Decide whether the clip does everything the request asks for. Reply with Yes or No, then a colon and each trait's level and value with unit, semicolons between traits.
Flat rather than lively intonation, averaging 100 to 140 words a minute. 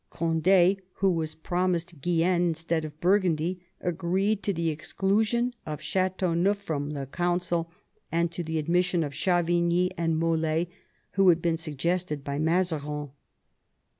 Yes: narrow, 2.3 semitones; slow, 135 wpm